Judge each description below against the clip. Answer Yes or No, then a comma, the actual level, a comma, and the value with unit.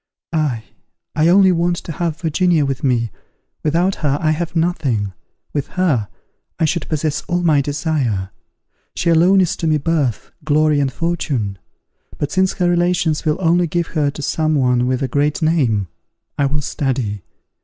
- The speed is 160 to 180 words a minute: Yes, average, 170 wpm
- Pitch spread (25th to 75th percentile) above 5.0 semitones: No, average, 3.8 semitones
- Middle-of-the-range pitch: Yes, medium, 155 Hz